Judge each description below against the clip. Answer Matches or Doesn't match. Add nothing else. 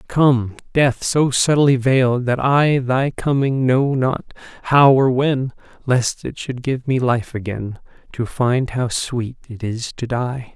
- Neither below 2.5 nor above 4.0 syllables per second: Matches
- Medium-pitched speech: Doesn't match